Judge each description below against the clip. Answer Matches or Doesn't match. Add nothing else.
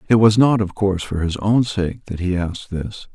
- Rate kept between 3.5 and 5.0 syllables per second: Doesn't match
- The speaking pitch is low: Matches